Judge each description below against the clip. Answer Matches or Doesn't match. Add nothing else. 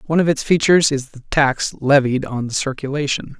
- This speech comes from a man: Matches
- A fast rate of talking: Doesn't match